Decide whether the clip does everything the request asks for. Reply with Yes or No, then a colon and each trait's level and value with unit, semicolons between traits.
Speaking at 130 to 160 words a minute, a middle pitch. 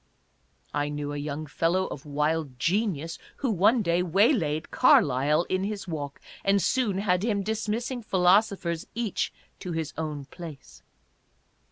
Yes: average, 145 wpm; medium, 170 Hz